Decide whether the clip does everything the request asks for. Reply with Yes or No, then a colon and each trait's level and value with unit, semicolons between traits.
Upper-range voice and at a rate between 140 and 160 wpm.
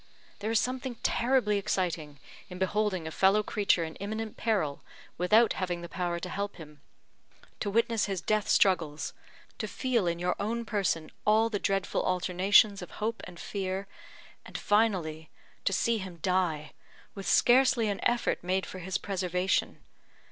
Yes: high, 195 Hz; average, 155 wpm